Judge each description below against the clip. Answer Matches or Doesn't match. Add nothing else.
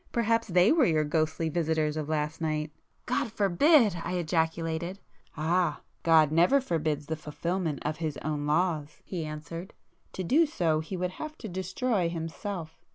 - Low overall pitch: Doesn't match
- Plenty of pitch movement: Doesn't match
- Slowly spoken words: Doesn't match